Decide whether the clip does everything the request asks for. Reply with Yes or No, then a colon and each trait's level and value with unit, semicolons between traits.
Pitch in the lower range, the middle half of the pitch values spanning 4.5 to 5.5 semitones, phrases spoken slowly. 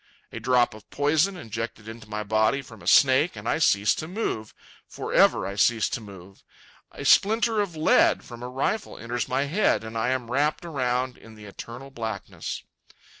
No: low, 120 Hz; average, 4.8 semitones; average, 180 wpm